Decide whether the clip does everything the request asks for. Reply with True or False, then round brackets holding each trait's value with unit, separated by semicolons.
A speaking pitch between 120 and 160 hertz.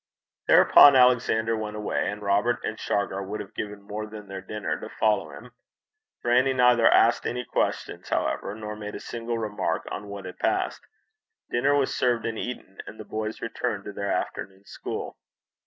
False (110 Hz)